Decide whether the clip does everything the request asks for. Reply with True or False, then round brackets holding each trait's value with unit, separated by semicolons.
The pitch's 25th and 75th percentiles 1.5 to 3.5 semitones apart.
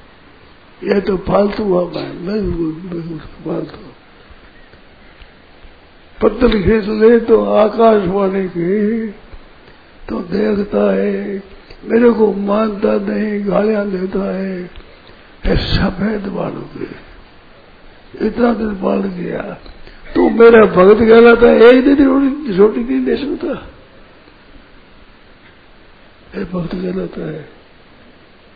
True (3.2 semitones)